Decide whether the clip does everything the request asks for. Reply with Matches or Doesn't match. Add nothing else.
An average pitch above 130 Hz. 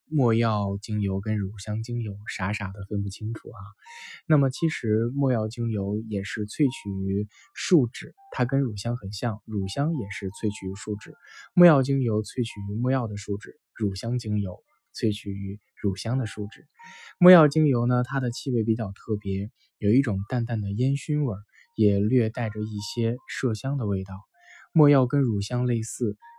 Doesn't match